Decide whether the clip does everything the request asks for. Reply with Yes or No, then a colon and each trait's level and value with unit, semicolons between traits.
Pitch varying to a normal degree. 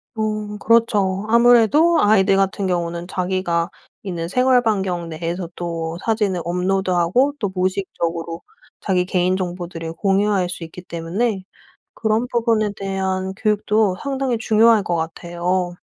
Yes: average, 3.6 semitones